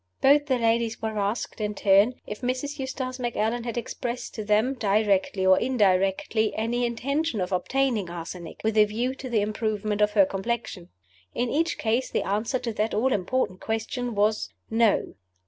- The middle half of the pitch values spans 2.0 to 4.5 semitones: Yes, average, 3.1 semitones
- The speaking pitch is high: Yes, high, 220 Hz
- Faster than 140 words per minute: Yes, average, 170 wpm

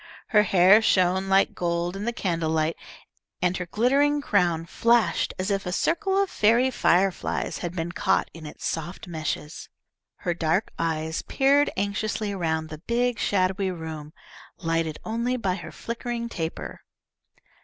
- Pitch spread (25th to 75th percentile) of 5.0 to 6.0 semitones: Yes, wide, 5.5 semitones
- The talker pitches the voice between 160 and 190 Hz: Yes, medium, 185 Hz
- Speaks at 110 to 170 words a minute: Yes, average, 145 wpm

